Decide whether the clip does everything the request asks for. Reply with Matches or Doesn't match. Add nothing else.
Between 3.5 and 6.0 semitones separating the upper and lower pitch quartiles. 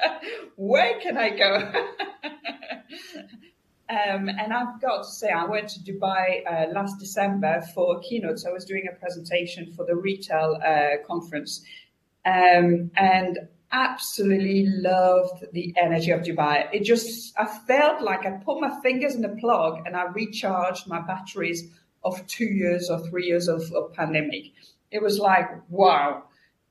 Matches